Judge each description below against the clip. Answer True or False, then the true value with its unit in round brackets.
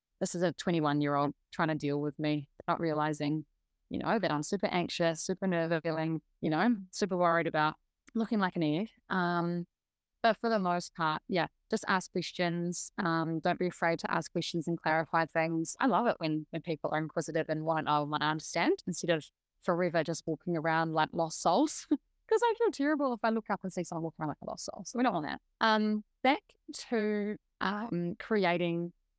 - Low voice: False (170 Hz)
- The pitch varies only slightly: False (4.0 semitones)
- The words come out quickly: True (210 wpm)